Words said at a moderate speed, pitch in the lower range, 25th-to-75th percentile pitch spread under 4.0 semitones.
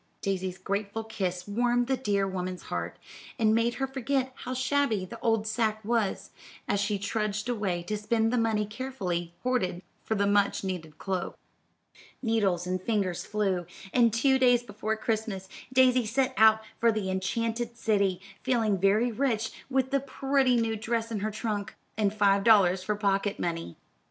No: average, 165 wpm; high, 215 Hz; average, 3.3 semitones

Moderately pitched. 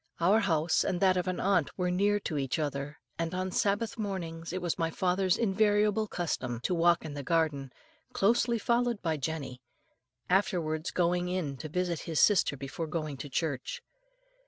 Yes: medium, 175 Hz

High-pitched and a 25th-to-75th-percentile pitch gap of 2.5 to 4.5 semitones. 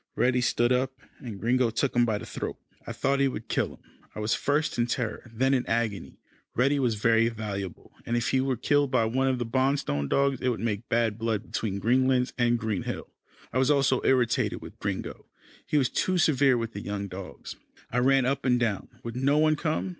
No: low, 125 Hz; average, 2.9 semitones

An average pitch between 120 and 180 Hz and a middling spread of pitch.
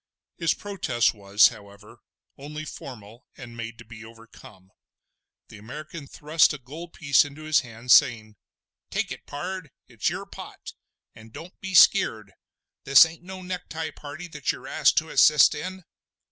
No: medium, 140 Hz; wide, 5.9 semitones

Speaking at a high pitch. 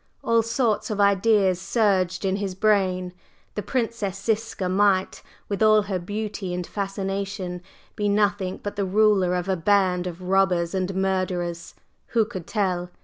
Yes: high, 195 Hz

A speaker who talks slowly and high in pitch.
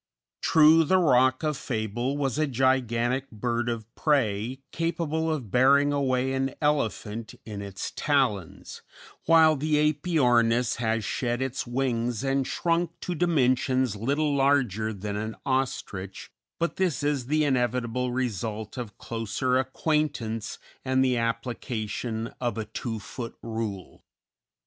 No: slow, 130 wpm; low, 125 Hz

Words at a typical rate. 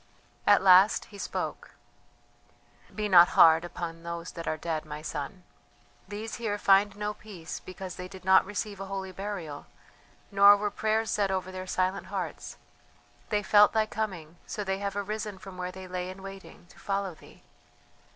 Yes: average, 170 wpm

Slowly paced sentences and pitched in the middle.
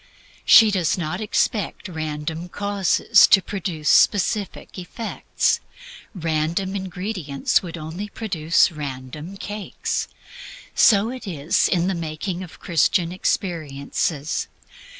Yes: slow, 105 wpm; medium, 175 Hz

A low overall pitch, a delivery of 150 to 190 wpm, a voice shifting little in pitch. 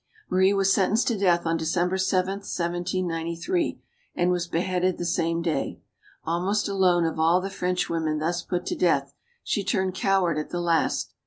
No: medium, 180 Hz; average, 175 wpm; narrow, 2.1 semitones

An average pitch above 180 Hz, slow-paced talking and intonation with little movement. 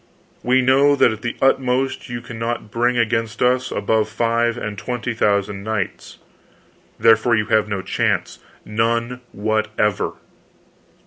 No: low, 115 Hz; slow, 125 wpm; narrow, 2.2 semitones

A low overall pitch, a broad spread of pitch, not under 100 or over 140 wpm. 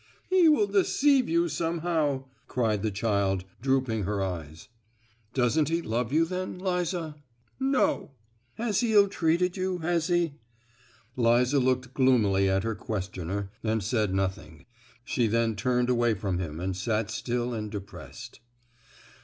Yes: low, 125 Hz; wide, 8.6 semitones; slow, 135 wpm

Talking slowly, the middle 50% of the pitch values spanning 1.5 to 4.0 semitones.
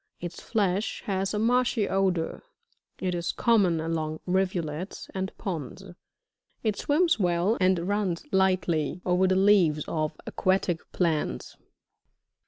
Yes: slow, 120 wpm; average, 2.8 semitones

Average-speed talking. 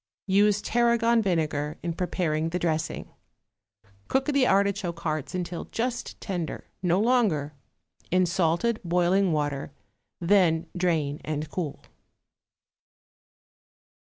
No: slow, 100 wpm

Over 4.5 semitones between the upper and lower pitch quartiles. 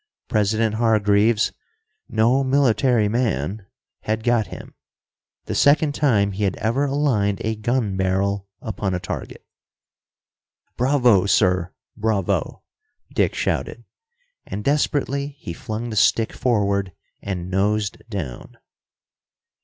No: average, 3.5 semitones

